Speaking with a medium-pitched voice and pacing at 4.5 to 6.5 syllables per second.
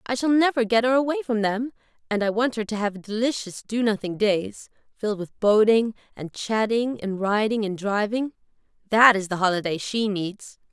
No: high, 220 Hz; 5.0 syllables/s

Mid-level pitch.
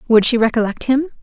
No: high, 240 Hz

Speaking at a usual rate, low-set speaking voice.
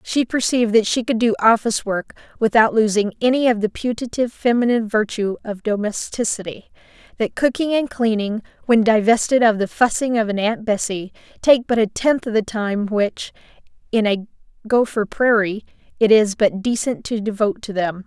No: average, 170 wpm; high, 220 Hz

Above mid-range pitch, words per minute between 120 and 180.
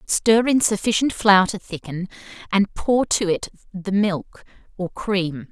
Yes: high, 195 Hz; average, 150 wpm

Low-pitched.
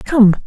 No: high, 230 Hz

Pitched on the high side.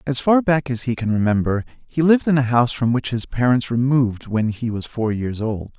No: low, 125 Hz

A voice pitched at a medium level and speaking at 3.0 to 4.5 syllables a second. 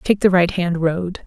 Yes: medium, 180 Hz; 4.1 syllables/s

